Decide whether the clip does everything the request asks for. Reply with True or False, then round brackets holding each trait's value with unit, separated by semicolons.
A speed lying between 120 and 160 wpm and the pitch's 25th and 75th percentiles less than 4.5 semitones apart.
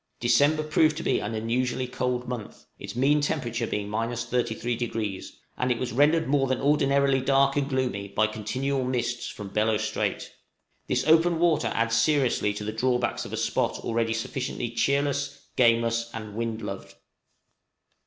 True (155 wpm; 3.4 semitones)